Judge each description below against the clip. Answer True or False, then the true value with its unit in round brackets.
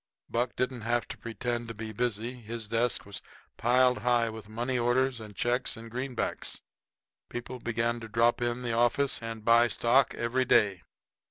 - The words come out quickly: False (175 wpm)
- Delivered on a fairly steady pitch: True (1.3 semitones)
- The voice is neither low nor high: False (120 Hz)